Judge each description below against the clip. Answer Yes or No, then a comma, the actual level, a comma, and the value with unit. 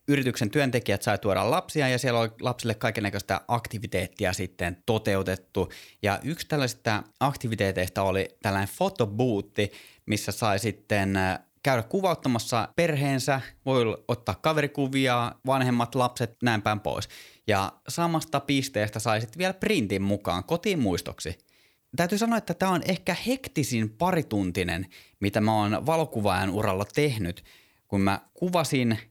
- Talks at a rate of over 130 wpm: No, average, 125 wpm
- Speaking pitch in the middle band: No, low, 115 Hz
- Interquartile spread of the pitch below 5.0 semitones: No, wide, 5.6 semitones